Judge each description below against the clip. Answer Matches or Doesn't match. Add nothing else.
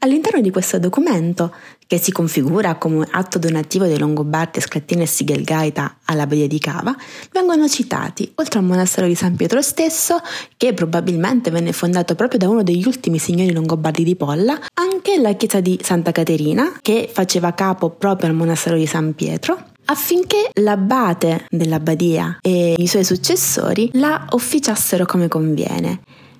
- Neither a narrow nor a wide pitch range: Doesn't match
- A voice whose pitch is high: Doesn't match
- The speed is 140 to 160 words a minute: Matches